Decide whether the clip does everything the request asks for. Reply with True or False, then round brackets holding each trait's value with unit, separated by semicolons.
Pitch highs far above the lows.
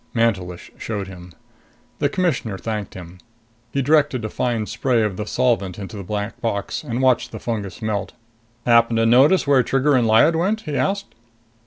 False (4.7 semitones)